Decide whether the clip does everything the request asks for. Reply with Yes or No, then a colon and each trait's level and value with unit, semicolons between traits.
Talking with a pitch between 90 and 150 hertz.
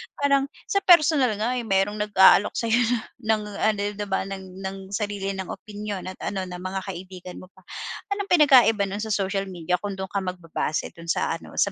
No: high, 200 Hz